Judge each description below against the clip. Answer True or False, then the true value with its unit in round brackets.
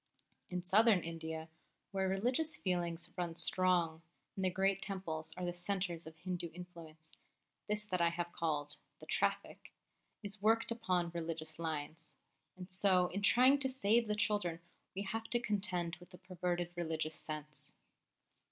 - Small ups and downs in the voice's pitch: False (3.2 semitones)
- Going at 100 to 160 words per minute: True (150 wpm)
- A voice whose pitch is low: False (180 Hz)